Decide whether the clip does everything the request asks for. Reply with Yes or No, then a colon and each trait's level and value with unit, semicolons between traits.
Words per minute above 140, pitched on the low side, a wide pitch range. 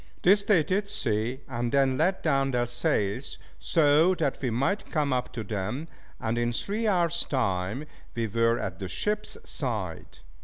Yes: average, 165 wpm; low, 130 Hz; wide, 6.3 semitones